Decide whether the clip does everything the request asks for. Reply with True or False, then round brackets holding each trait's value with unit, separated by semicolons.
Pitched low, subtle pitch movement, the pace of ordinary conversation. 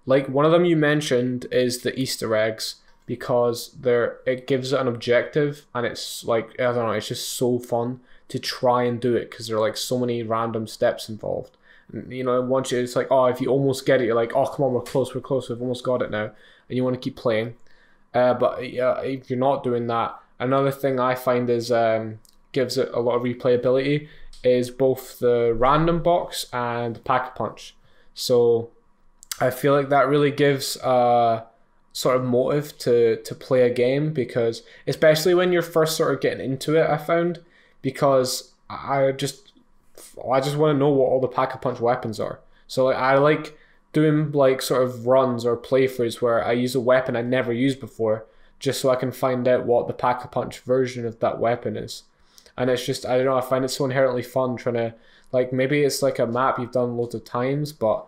False (125 Hz; 1.9 semitones; 215 wpm)